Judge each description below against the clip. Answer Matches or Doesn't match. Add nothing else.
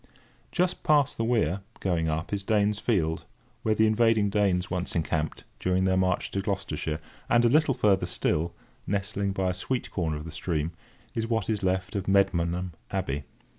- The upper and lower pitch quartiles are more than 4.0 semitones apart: Doesn't match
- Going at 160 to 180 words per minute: Matches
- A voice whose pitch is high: Doesn't match